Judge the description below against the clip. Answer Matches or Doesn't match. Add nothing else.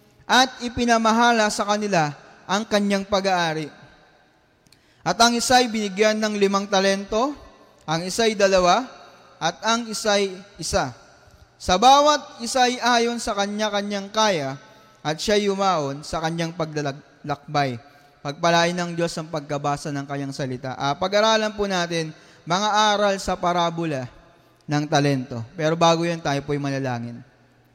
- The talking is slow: Doesn't match